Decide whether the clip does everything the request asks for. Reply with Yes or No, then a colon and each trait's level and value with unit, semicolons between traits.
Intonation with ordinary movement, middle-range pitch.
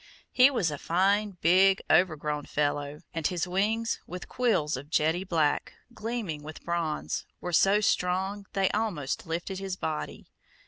Yes: average, 4.1 semitones; medium, 180 Hz